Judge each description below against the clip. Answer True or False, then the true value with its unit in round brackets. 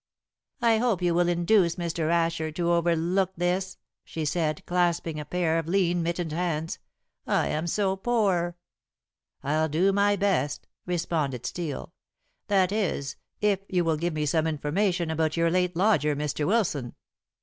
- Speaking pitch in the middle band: True (170 Hz)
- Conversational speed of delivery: True (150 wpm)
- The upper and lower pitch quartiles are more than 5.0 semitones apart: False (2.7 semitones)